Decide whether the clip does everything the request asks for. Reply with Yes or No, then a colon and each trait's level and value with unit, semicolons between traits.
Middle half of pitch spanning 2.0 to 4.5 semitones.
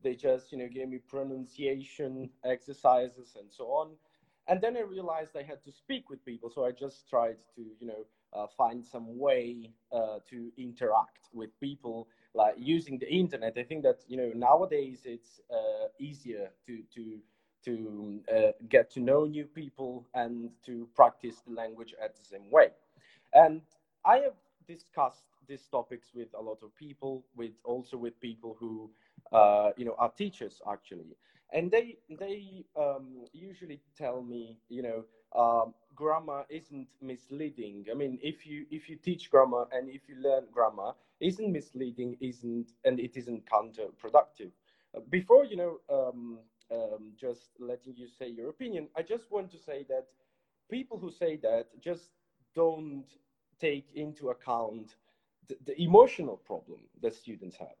No: average, 5.0 semitones